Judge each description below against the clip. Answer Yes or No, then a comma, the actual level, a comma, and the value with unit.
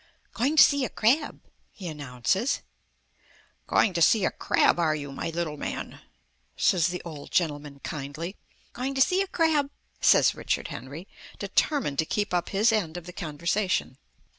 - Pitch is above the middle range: No, medium, 175 Hz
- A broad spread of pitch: Yes, wide, 7.4 semitones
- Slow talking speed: No, average, 165 wpm